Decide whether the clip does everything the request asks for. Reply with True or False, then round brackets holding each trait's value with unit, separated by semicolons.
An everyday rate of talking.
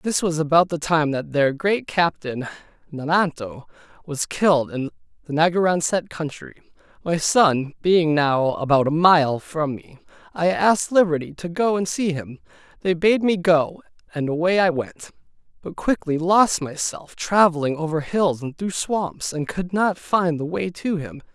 True (165 wpm)